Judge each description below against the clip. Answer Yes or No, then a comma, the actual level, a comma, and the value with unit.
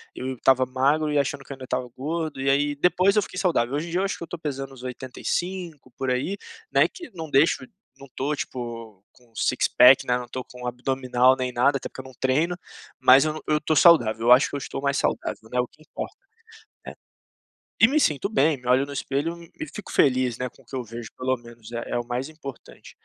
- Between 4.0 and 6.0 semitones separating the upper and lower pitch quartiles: No, average, 3.6 semitones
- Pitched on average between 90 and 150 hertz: Yes, low, 135 Hz